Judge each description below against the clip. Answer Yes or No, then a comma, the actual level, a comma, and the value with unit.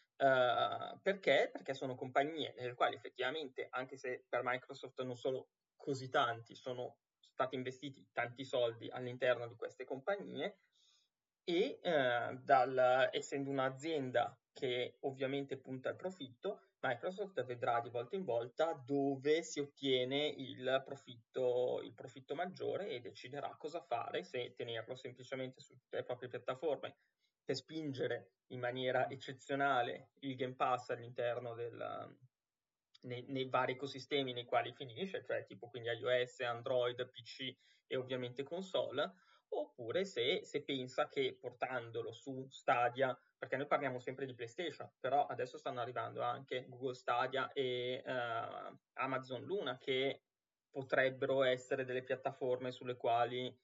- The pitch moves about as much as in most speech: No, narrow, 1.9 semitones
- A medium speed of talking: Yes, average, 130 wpm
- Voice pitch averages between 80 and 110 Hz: No, low, 130 Hz